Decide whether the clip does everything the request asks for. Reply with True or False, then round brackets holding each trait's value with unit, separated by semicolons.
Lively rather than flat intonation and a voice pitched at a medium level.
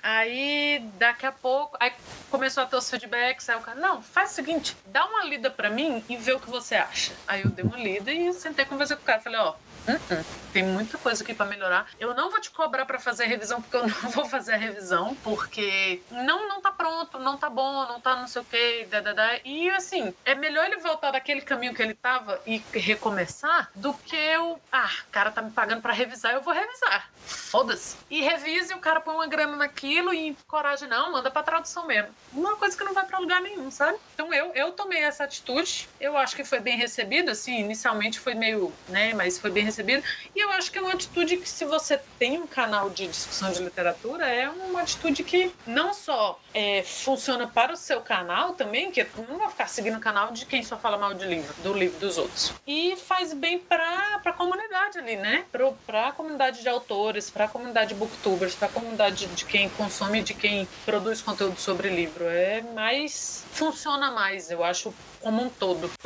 False (6.6 semitones; 255 Hz)